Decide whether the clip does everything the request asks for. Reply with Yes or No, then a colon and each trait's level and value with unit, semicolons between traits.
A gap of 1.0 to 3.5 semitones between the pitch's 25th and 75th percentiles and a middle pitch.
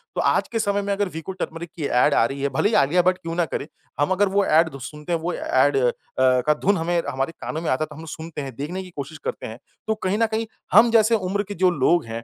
No: average, 5.1 semitones; medium, 165 Hz